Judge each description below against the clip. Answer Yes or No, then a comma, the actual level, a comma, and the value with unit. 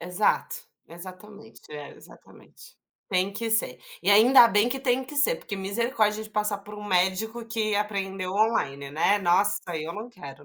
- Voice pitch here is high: Yes, high, 205 Hz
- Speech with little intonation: No, average, 3.3 semitones